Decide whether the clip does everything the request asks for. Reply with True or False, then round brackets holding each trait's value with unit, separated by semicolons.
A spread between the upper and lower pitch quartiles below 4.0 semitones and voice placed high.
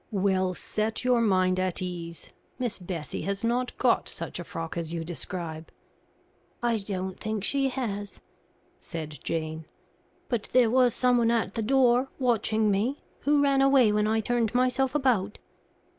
False (5.1 semitones; 215 Hz)